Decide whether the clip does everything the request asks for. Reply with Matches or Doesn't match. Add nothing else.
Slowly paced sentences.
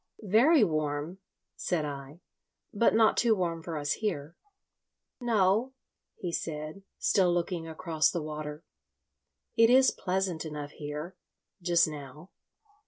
Matches